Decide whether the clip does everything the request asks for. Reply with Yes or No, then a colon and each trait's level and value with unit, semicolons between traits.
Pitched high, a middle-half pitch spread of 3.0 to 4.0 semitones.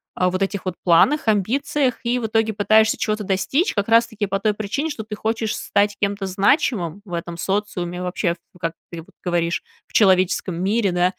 Yes: high, 200 Hz; average, 3.3 semitones